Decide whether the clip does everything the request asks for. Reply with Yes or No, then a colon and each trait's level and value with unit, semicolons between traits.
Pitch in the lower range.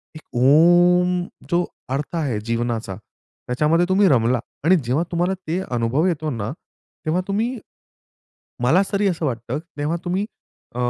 No: medium, 160 Hz